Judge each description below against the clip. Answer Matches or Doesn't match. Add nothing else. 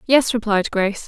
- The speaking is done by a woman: Matches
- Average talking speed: Matches